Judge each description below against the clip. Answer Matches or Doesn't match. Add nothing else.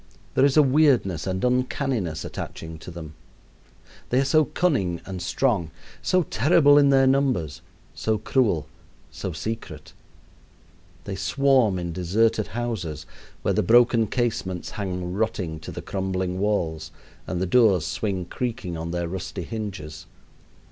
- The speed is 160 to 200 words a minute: Doesn't match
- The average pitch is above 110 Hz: Doesn't match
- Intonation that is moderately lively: Doesn't match